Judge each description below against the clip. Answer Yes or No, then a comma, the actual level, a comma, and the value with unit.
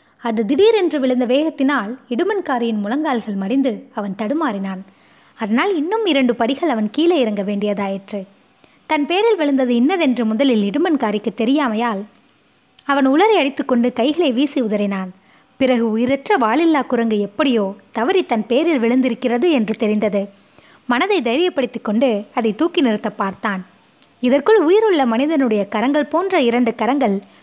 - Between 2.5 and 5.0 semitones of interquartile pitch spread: No, wide, 5.4 semitones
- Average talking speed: Yes, average, 120 wpm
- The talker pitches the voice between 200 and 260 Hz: Yes, very high, 250 Hz